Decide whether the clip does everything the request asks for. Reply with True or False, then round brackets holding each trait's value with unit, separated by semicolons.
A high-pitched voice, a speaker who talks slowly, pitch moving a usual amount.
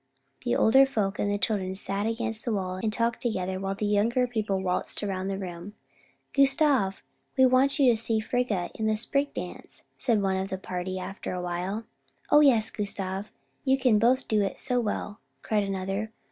False (210 Hz; 190 wpm; 3.6 semitones)